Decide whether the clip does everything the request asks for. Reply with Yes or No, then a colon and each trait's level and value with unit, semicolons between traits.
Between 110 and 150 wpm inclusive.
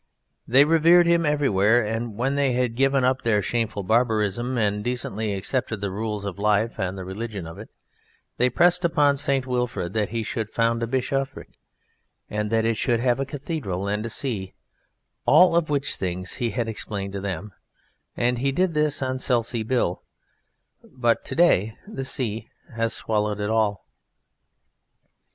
No: average, 165 wpm